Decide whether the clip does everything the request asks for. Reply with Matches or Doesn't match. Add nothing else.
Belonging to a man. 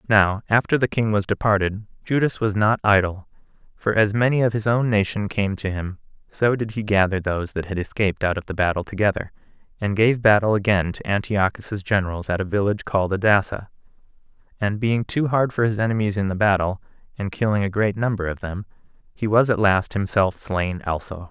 Matches